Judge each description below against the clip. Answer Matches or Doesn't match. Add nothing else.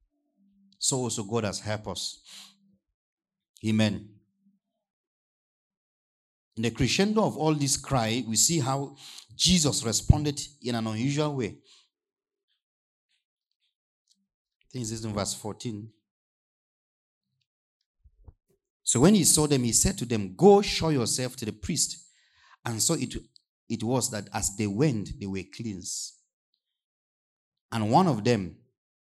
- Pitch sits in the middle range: Doesn't match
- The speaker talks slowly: Matches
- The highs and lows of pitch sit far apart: Matches